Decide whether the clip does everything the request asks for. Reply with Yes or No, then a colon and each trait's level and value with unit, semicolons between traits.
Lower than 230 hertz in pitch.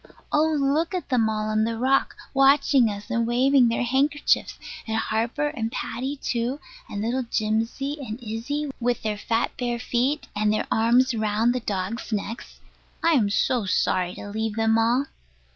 No: high, 235 Hz